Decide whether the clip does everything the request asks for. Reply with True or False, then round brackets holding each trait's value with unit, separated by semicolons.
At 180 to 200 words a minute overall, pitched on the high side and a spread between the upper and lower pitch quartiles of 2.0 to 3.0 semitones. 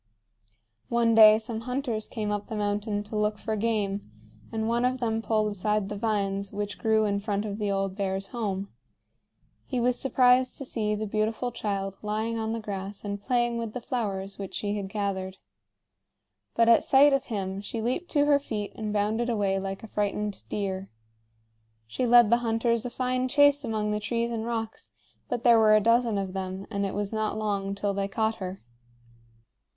True (190 wpm; 215 Hz; 2.6 semitones)